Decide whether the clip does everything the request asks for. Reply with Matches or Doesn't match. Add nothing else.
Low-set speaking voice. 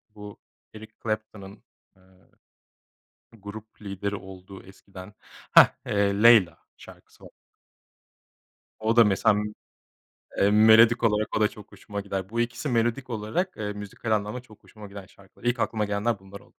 Matches